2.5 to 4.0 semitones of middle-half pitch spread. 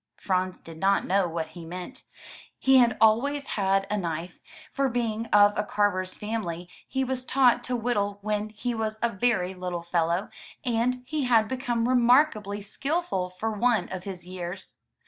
No: average, 4.8 semitones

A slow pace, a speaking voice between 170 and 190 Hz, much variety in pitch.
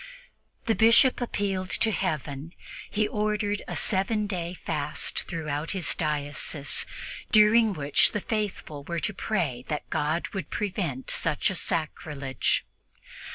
Yes: slow, 125 wpm; medium, 185 Hz; wide, 5.9 semitones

